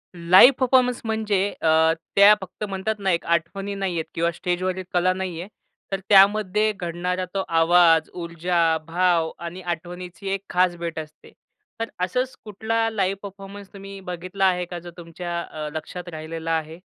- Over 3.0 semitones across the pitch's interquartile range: No, average, 2.7 semitones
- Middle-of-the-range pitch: Yes, medium, 180 Hz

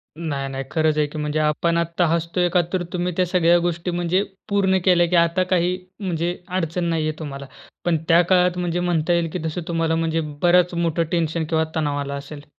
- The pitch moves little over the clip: Yes, narrow, 1.9 semitones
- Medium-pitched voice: Yes, medium, 170 Hz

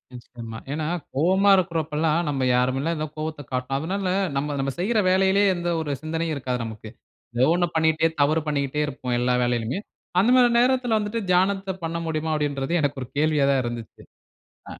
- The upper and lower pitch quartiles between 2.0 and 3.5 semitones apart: No, average, 5.2 semitones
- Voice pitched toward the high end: No, medium, 155 Hz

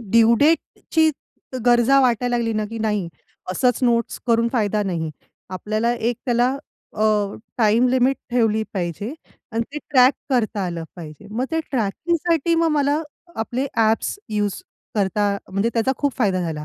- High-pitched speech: Yes, high, 230 Hz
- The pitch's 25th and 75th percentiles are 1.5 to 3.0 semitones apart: No, average, 3.6 semitones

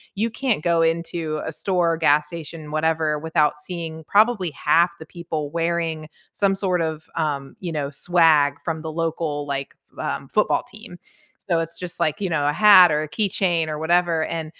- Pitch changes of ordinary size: No, narrow, 2.1 semitones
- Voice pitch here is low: No, medium, 165 Hz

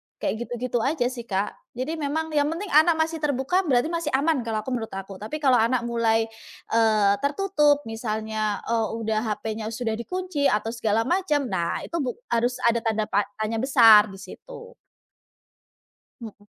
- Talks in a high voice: Yes, high, 235 Hz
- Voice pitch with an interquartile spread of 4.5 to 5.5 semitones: Yes, average, 5.2 semitones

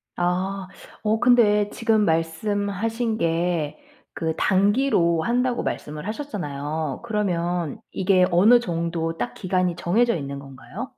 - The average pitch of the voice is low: No, medium, 185 Hz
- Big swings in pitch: No, average, 4.8 semitones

